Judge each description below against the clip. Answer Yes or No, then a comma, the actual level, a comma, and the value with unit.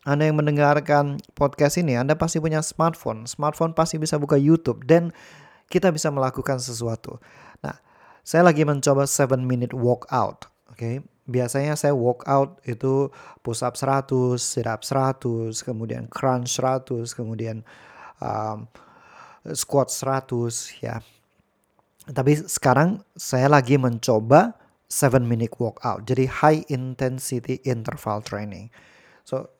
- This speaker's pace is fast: No, average, 130 wpm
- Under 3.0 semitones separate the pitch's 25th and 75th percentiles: No, average, 3.3 semitones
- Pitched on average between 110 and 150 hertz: Yes, low, 135 Hz